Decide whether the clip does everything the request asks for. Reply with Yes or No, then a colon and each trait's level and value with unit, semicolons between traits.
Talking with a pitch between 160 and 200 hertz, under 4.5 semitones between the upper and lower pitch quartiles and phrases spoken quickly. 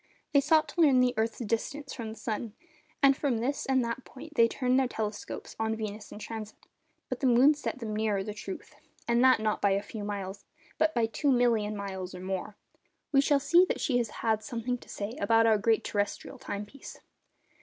No: high, 230 Hz; average, 3.7 semitones; fast, 210 wpm